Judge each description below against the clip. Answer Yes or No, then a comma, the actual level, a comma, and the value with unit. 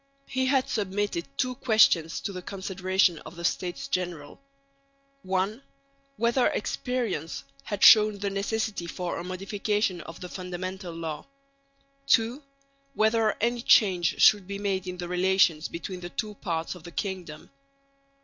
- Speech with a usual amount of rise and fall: Yes, average, 3.3 semitones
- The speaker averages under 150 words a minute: Yes, average, 140 wpm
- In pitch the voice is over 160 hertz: Yes, high, 190 Hz